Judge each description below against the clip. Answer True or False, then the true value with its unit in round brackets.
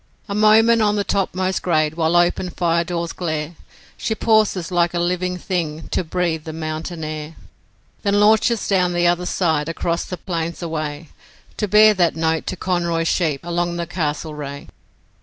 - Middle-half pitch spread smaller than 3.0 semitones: True (2.5 semitones)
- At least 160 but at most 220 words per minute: True (165 wpm)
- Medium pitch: True (175 Hz)